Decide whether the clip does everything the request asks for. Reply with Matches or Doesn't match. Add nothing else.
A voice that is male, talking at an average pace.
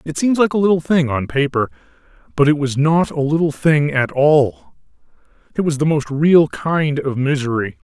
Matches